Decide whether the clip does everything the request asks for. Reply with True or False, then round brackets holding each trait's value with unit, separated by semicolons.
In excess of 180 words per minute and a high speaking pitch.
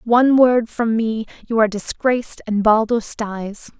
False (160 wpm; 225 Hz)